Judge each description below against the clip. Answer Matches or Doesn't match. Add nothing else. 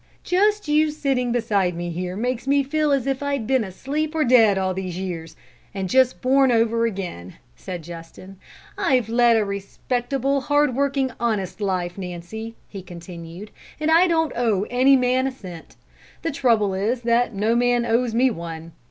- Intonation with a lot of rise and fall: Matches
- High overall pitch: Matches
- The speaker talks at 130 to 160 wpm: Doesn't match